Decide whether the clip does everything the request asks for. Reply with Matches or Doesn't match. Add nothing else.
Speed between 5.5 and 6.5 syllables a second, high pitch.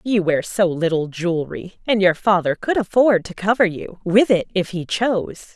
Doesn't match